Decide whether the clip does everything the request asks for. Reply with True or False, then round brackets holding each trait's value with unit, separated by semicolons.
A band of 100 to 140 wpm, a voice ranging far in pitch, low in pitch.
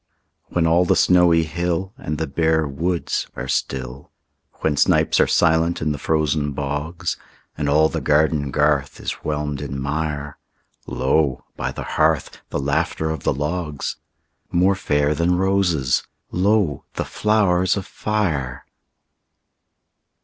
False (135 wpm; 3.4 semitones; 80 Hz)